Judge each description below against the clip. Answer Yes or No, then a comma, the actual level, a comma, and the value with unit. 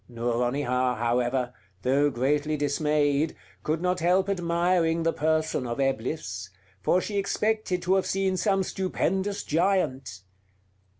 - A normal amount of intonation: No, wide, 6.2 semitones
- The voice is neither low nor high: Yes, medium, 155 Hz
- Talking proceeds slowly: Yes, slow, 120 wpm